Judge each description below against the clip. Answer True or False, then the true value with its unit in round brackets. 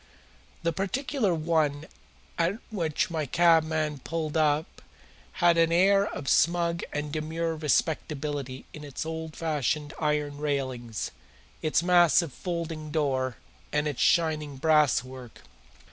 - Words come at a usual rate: False (115 wpm)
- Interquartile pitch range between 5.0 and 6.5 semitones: False (2.4 semitones)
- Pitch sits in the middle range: True (155 Hz)